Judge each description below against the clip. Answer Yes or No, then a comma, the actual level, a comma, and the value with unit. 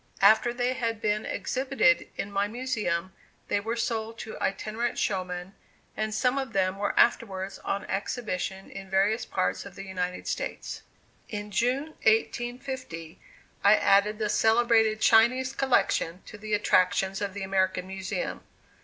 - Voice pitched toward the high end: Yes, high, 210 Hz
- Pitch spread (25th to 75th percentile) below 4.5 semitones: Yes, average, 3.5 semitones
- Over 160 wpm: No, average, 145 wpm